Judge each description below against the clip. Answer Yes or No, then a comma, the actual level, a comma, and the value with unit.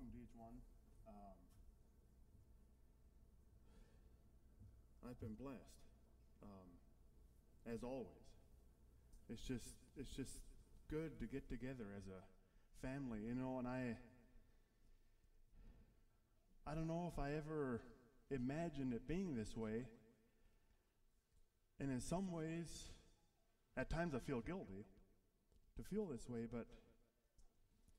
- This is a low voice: Yes, low, 115 Hz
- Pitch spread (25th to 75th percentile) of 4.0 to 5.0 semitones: Yes, average, 4.7 semitones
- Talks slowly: Yes, slow, 105 wpm